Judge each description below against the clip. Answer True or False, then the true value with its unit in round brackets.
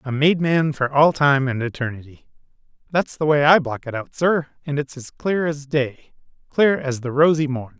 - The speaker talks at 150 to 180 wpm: False (190 wpm)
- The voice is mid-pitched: True (145 Hz)